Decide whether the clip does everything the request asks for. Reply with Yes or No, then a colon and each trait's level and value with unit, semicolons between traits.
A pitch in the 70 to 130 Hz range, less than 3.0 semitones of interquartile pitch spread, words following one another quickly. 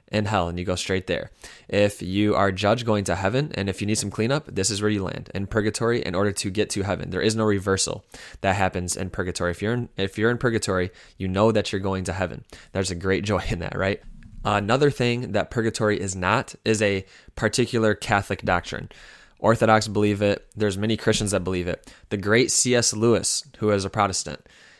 Yes: low, 105 Hz; narrow, 2.6 semitones; fast, 220 wpm